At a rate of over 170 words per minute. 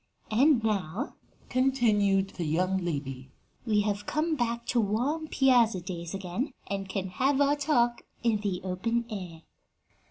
No: average, 145 wpm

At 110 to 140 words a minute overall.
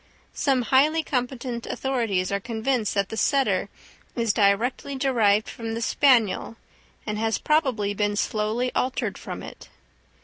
Yes: slow, 135 wpm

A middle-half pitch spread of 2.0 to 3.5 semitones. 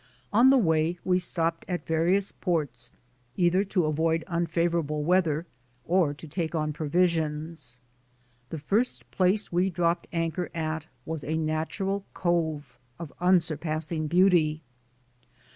Yes: narrow, 2.5 semitones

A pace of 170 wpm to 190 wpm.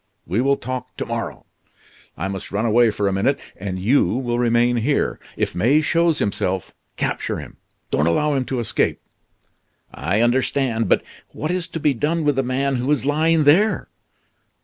Yes: average, 175 wpm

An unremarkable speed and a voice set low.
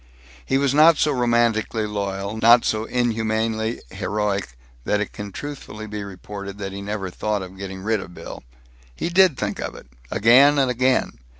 Yes: average, 175 wpm; low, 110 Hz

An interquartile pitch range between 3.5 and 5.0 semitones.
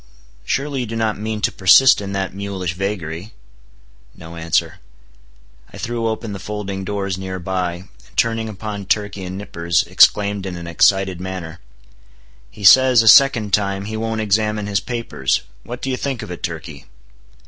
No: average, 3.1 semitones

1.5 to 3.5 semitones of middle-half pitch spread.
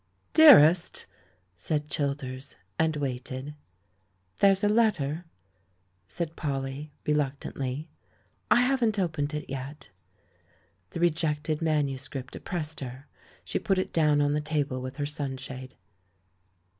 Yes: average, 3.2 semitones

